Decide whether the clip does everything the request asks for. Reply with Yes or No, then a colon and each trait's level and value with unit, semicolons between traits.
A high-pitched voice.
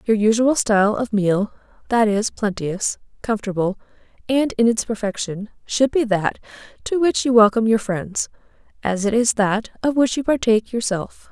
Yes: high, 220 Hz